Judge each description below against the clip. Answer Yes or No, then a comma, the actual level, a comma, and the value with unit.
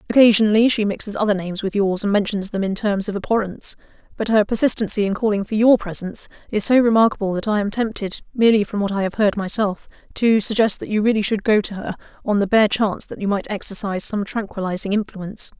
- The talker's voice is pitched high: Yes, high, 205 Hz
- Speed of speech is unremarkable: No, fast, 215 wpm